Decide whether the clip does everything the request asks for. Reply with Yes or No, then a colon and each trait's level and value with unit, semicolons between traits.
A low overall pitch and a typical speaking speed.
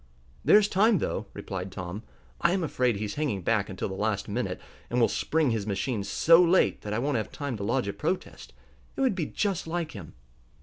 No: low, 120 Hz; fast, 210 wpm